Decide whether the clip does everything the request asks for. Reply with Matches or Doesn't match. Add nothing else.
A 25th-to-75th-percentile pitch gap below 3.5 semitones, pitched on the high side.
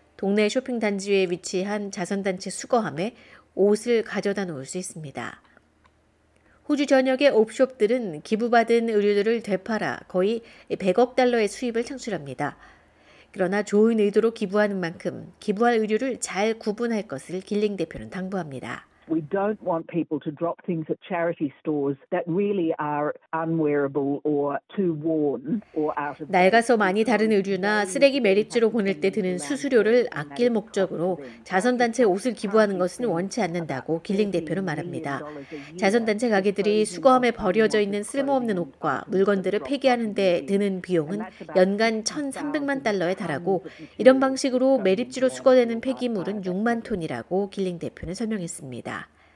Doesn't match